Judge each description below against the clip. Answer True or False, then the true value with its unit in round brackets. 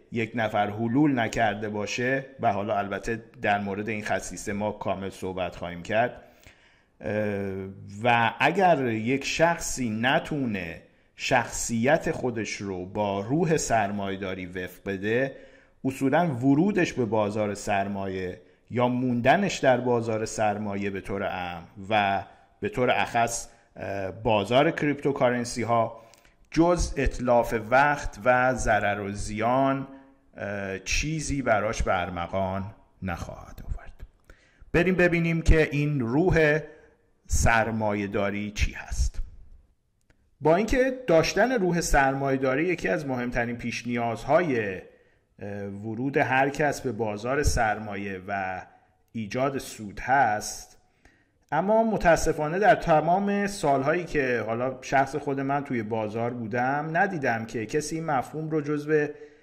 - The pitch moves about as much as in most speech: False (6.1 semitones)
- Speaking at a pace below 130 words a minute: True (110 wpm)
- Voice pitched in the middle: False (115 Hz)